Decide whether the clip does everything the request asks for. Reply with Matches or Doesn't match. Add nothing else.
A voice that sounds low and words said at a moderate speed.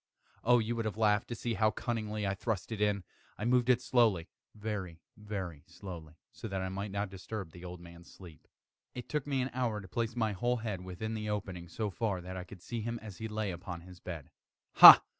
Doesn't match